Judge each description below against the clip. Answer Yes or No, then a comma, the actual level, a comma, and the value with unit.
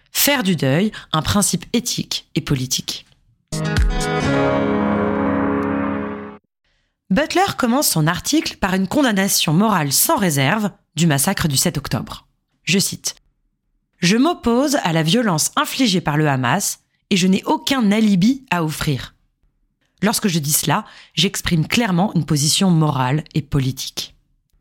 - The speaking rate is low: Yes, slow, 125 wpm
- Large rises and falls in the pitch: Yes, wide, 6.8 semitones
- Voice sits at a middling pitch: Yes, medium, 175 Hz